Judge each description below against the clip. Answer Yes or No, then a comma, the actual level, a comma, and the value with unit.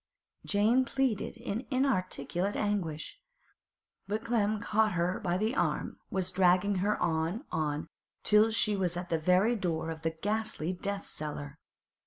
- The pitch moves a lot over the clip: No, average, 4.1 semitones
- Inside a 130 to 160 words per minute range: Yes, average, 150 wpm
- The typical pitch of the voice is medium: No, high, 195 Hz